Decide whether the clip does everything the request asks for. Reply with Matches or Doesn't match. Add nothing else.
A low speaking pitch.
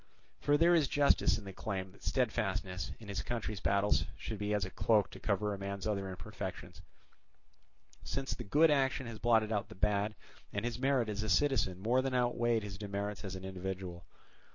Matches